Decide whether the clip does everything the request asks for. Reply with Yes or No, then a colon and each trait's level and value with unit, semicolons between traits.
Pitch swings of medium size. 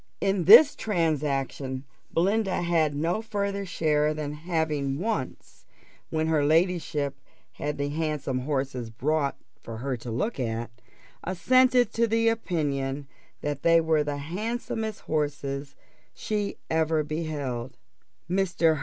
Yes: average, 4.6 semitones